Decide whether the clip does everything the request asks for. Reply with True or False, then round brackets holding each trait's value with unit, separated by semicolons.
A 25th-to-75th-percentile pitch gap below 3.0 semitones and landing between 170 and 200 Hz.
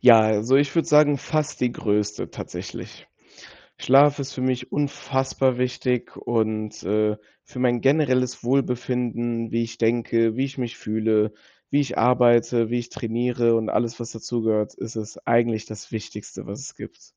False (2.4 semitones; 120 Hz)